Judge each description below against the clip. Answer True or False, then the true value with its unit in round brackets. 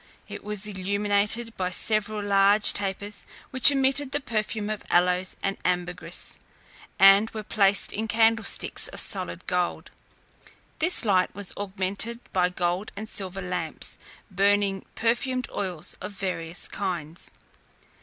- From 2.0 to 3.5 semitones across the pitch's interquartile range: True (2.8 semitones)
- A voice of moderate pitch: False (200 Hz)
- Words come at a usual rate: False (125 wpm)